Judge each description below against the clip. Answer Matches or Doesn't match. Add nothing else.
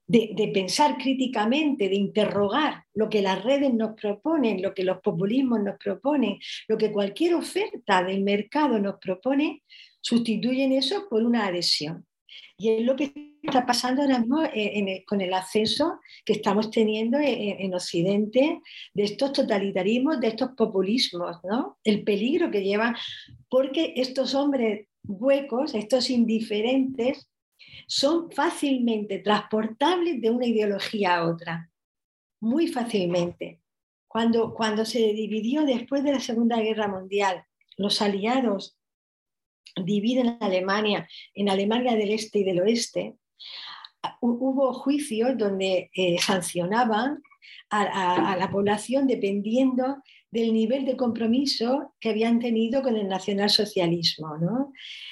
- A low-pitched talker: Doesn't match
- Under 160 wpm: Matches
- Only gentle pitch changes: Doesn't match